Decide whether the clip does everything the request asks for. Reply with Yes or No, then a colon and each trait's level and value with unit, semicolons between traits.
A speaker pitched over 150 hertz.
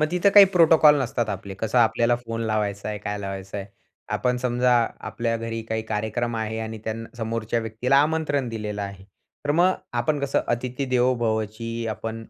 No: low, 115 Hz